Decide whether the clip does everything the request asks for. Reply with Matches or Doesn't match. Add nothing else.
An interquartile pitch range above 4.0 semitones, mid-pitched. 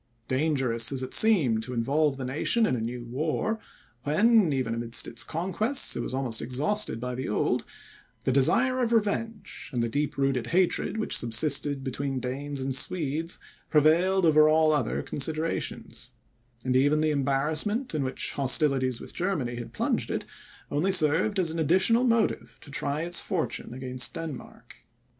Matches